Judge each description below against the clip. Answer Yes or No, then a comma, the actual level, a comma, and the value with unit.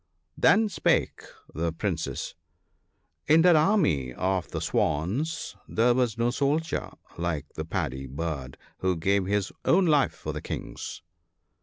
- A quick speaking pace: No, average, 145 wpm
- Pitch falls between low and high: No, low, 100 Hz